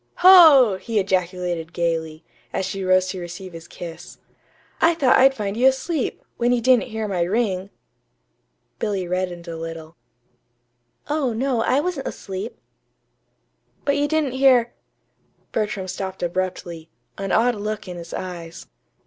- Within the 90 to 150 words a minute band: Yes, average, 145 wpm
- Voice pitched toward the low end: No, high, 195 Hz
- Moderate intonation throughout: No, wide, 6.0 semitones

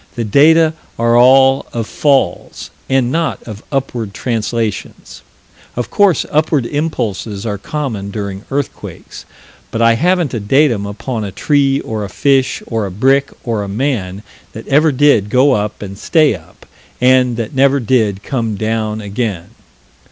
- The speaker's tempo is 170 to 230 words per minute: No, average, 150 wpm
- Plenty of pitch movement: No, average, 4.7 semitones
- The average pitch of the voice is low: Yes, low, 120 Hz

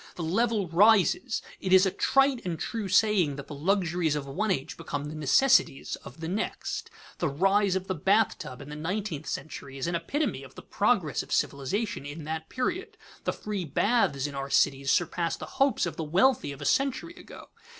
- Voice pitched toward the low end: No, medium, 175 Hz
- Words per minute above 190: Yes, average, 200 wpm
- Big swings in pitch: Yes, wide, 6.3 semitones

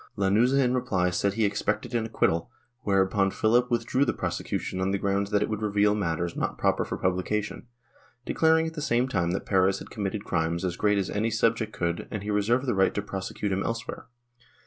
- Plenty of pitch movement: No, average, 3.1 semitones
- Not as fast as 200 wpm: No, fast, 205 wpm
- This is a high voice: No, low, 105 Hz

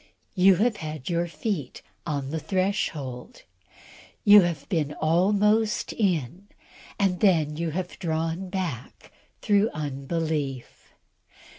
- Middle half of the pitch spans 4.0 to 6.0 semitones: Yes, average, 4.3 semitones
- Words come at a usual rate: No, slow, 110 wpm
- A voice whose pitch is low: No, medium, 170 Hz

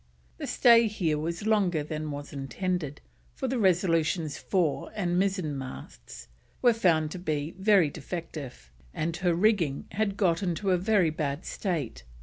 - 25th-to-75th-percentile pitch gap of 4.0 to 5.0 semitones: Yes, average, 4.3 semitones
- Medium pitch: Yes, medium, 175 Hz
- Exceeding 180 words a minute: No, average, 150 wpm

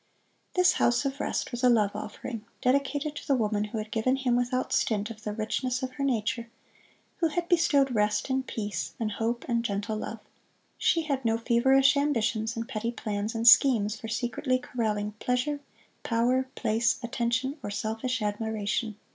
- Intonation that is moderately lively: Yes, average, 3.2 semitones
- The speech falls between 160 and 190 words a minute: Yes, average, 170 wpm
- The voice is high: Yes, high, 235 Hz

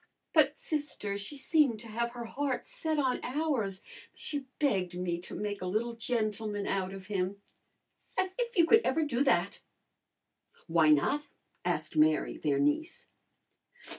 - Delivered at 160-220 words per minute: No, average, 150 wpm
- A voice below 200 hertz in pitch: No, high, 225 Hz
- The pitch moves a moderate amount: No, wide, 7.6 semitones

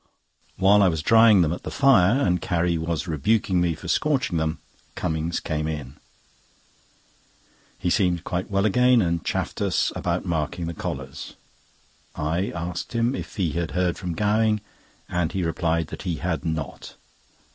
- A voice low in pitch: Yes, very low, 85 Hz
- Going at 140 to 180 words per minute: Yes, average, 160 wpm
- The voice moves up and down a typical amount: Yes, average, 3.8 semitones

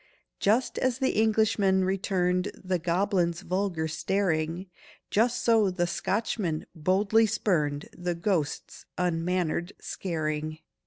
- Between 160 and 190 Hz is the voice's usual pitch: Yes, medium, 185 Hz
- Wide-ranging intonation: No, average, 3.3 semitones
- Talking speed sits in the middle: No, slow, 105 wpm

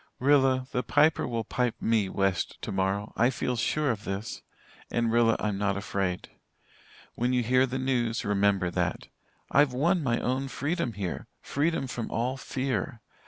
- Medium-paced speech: Yes, average, 160 wpm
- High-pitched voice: No, low, 120 Hz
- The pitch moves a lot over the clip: No, average, 4.3 semitones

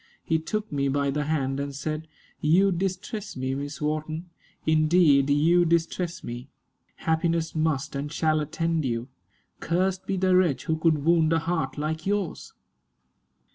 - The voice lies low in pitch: No, medium, 160 Hz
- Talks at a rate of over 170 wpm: No, average, 150 wpm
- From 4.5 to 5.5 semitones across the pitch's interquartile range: No, average, 3.1 semitones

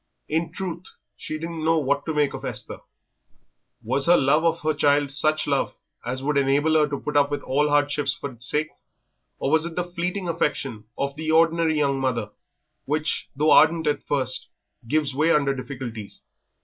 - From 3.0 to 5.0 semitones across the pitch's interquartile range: No, narrow, 2.5 semitones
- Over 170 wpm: Yes, average, 185 wpm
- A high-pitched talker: No, medium, 150 Hz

